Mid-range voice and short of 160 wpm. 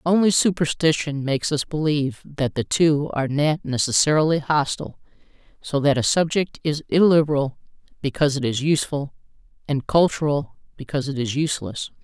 Yes: medium, 150 Hz; slow, 135 wpm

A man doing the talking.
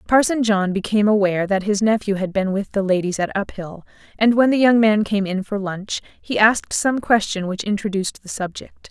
No: female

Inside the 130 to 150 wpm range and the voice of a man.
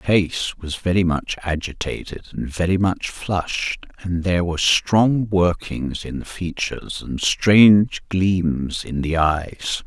Yes: average, 145 wpm; male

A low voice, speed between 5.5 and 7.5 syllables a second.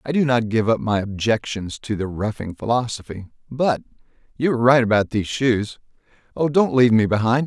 Yes: low, 115 Hz; 5.6 syllables/s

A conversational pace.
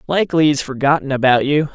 Yes: average, 170 wpm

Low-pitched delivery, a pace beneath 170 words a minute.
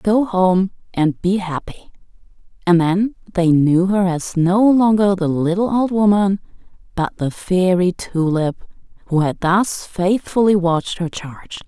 No: medium, 185 Hz; average, 145 wpm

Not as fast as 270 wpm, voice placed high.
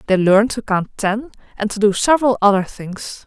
Yes: average, 200 wpm; high, 215 Hz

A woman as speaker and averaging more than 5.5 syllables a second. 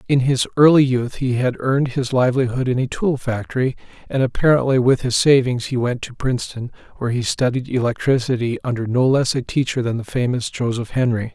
No: male; 5.8 syllables/s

